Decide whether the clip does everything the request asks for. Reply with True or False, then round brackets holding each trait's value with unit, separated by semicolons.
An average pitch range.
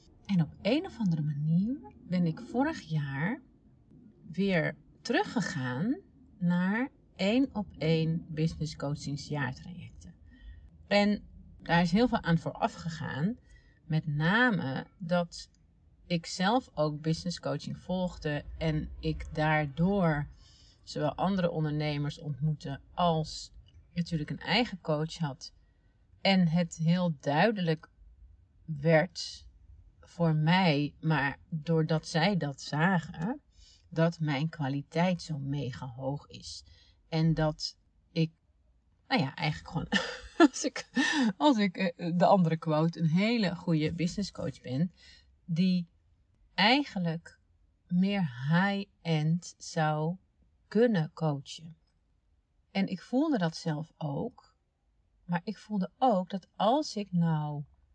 True (4.2 semitones)